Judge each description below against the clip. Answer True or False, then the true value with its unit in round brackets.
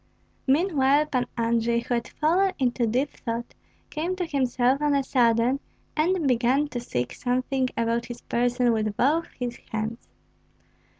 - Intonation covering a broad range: False (3.5 semitones)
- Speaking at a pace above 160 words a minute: False (145 wpm)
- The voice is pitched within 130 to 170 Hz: False (250 Hz)